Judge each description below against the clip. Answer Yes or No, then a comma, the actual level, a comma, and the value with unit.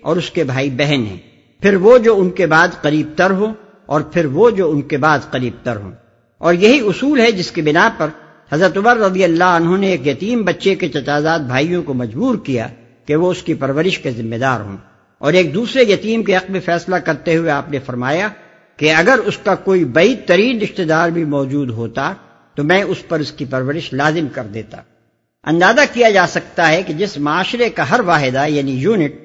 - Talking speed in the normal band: No, fast, 215 wpm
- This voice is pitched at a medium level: Yes, medium, 165 Hz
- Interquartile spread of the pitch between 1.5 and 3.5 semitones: No, average, 5.2 semitones